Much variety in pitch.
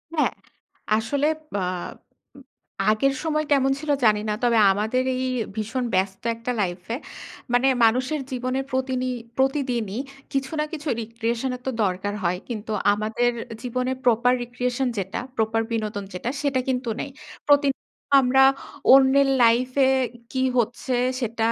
No: average, 3.2 semitones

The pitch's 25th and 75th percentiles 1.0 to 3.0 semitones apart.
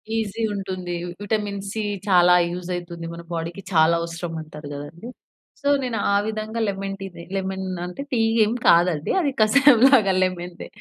No: average, 4.0 semitones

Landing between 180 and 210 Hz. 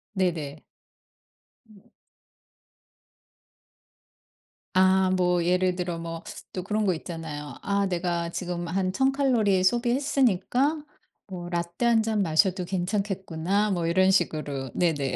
Yes: medium, 185 Hz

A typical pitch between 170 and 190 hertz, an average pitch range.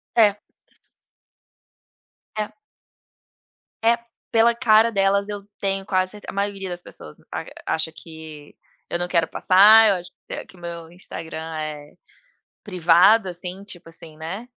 Yes: medium, 185 Hz; average, 3.7 semitones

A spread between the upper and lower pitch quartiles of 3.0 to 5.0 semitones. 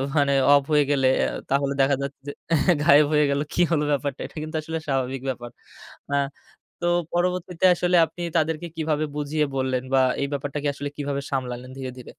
No: narrow, 2.5 semitones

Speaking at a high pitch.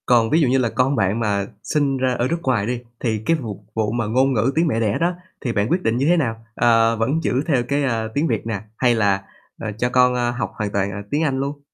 No: low, 120 Hz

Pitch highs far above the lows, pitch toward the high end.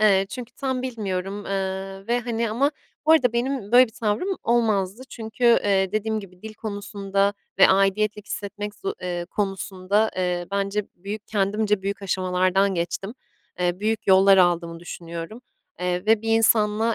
No: narrow, 2.6 semitones; high, 205 Hz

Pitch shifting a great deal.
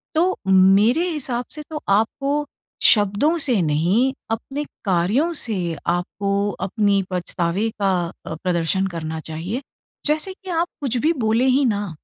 Yes: wide, 6.9 semitones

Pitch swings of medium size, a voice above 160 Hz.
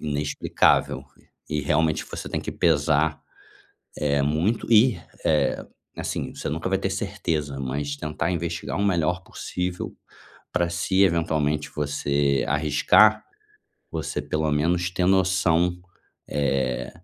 No: average, 3.6 semitones; very low, 80 Hz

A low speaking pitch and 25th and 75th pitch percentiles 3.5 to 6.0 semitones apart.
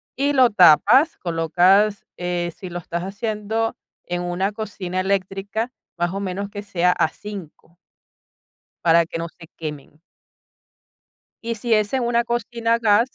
No: high, 200 Hz; average, 4.2 semitones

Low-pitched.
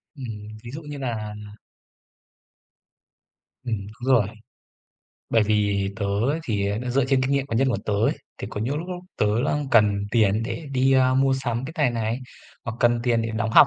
Yes: low, 120 Hz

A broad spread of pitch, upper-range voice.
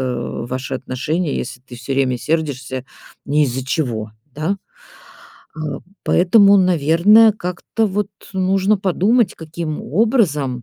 No: wide, 6.6 semitones; medium, 155 Hz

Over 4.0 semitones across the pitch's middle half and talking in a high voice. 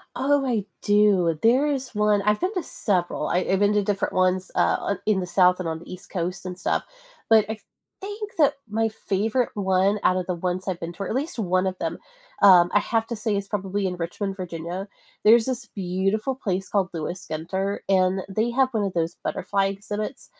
No: average, 3.1 semitones; high, 195 Hz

